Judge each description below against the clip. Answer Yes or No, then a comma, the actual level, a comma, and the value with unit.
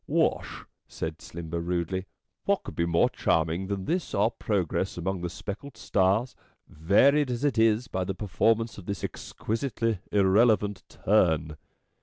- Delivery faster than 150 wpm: No, average, 145 wpm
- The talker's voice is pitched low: Yes, low, 100 Hz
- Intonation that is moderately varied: Yes, average, 4.6 semitones